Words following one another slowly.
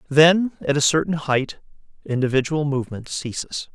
Yes: slow, 130 wpm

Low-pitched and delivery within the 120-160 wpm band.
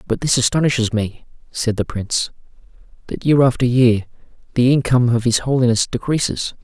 Yes: low, 125 Hz; average, 155 wpm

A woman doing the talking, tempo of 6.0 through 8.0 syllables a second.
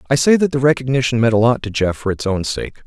No: male; 6.4 syllables/s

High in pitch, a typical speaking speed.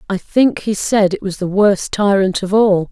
No: high, 200 Hz; fast, 225 wpm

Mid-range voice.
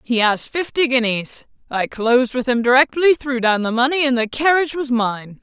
No: very high, 255 Hz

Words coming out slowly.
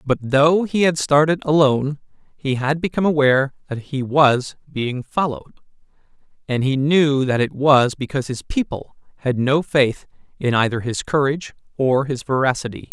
No: average, 160 wpm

